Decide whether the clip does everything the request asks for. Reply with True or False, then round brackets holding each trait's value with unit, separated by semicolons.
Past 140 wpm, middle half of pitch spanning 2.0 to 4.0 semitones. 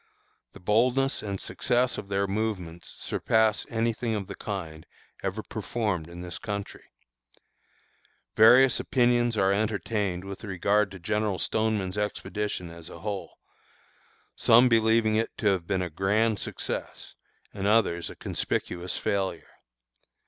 False (135 wpm; 2.9 semitones)